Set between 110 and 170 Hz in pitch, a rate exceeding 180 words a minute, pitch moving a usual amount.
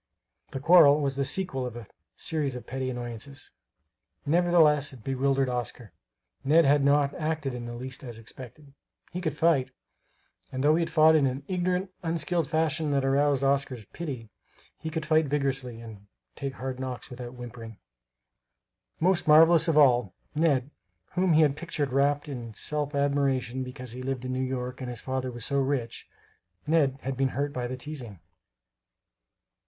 No: low, 135 Hz; average, 165 wpm; average, 3.2 semitones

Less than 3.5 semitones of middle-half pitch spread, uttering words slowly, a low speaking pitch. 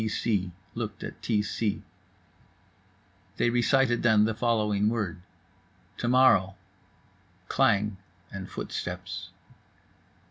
Yes: average, 2.7 semitones; slow, 100 wpm; low, 110 Hz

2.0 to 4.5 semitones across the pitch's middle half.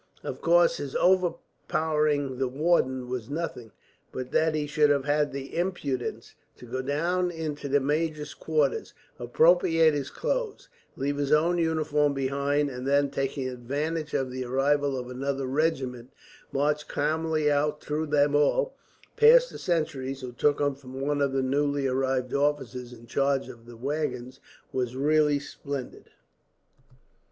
Yes: average, 2.8 semitones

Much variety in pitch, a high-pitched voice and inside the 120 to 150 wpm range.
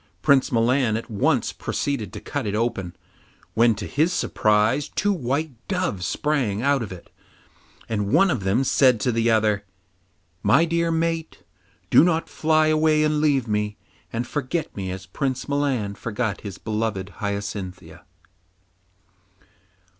No: wide, 6.4 semitones; low, 120 Hz; average, 145 wpm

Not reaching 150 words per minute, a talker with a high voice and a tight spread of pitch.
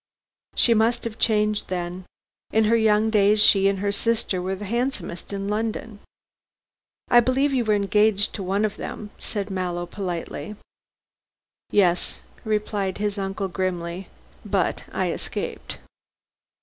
Yes: average, 140 wpm; high, 205 Hz; narrow, 2.3 semitones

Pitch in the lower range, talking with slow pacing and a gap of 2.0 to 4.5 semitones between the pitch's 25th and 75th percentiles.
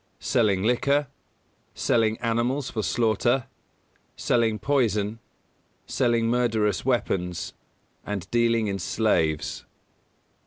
Yes: low, 115 Hz; slow, 85 wpm; narrow, 2.5 semitones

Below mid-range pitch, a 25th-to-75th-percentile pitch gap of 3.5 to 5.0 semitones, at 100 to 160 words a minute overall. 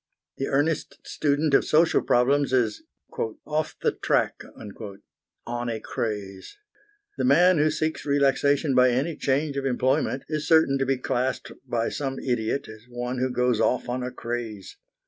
No: low, 130 Hz; average, 2.8 semitones; average, 155 wpm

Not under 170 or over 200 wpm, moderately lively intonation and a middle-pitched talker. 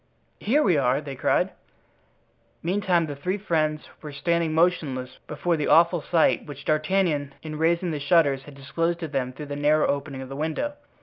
Yes: average, 180 wpm; average, 3.1 semitones; medium, 155 Hz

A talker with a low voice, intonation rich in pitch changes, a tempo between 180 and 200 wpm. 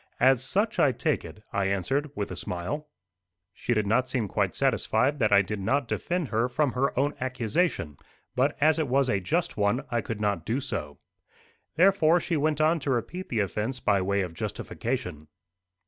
Yes: low, 125 Hz; wide, 6.0 semitones; average, 190 wpm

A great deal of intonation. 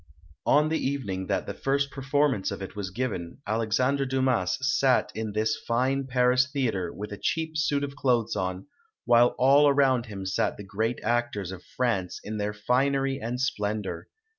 No: average, 4.7 semitones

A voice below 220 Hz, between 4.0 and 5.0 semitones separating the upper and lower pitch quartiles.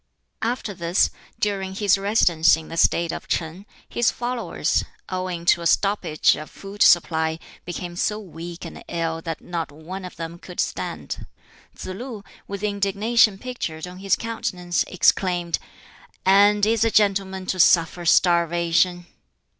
No: medium, 185 Hz; average, 3.0 semitones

